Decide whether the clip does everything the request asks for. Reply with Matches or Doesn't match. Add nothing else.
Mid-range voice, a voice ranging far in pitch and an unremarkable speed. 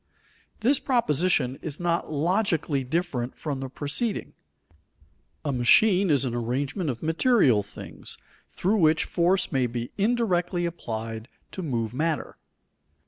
Doesn't match